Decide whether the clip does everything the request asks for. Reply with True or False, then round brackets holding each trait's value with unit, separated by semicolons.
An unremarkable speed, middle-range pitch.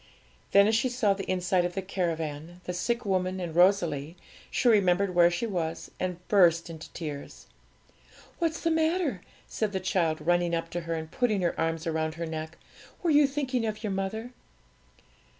True (180 wpm; 180 Hz)